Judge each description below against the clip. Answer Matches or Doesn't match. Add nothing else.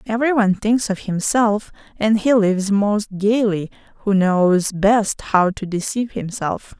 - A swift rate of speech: Doesn't match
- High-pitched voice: Matches